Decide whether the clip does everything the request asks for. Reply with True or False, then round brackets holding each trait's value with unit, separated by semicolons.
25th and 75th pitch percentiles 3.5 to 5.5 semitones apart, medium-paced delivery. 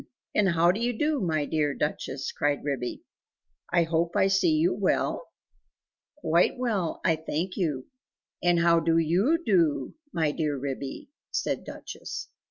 True (4.5 semitones; 150 wpm)